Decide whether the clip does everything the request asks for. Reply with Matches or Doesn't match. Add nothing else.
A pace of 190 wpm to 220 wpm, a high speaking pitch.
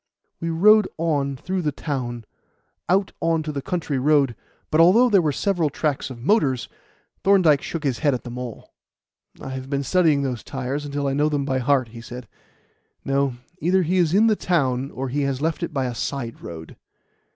Doesn't match